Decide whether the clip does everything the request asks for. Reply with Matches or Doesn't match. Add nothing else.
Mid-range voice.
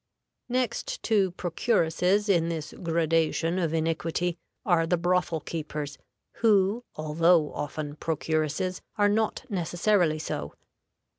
Matches